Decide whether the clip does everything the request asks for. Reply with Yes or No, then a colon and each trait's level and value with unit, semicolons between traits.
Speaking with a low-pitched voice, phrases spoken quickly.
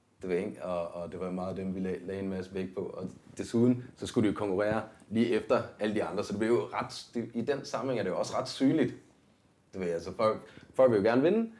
Yes: low, 100 Hz; fast, 260 wpm